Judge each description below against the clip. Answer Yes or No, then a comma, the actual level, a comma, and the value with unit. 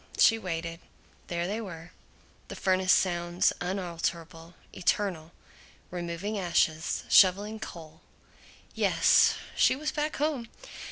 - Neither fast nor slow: No, slow, 105 wpm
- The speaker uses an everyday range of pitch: Yes, average, 3.5 semitones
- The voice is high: No, medium, 180 Hz